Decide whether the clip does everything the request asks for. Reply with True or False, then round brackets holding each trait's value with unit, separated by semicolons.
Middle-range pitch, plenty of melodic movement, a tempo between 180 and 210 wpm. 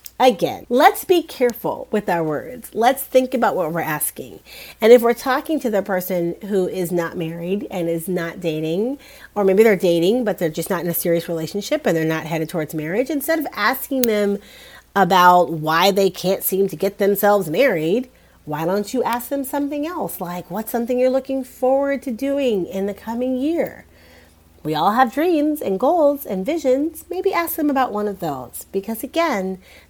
False (205 Hz; 7.1 semitones; 190 wpm)